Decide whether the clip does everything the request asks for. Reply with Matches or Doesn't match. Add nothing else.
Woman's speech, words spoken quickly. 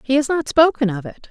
Matches